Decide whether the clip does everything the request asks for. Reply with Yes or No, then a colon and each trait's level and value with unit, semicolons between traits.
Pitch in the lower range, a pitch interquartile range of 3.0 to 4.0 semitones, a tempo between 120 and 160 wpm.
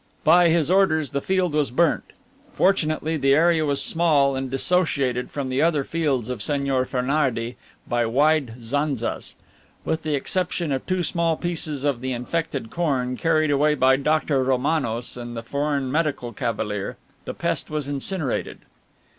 No: medium, 145 Hz; average, 3.7 semitones; average, 155 wpm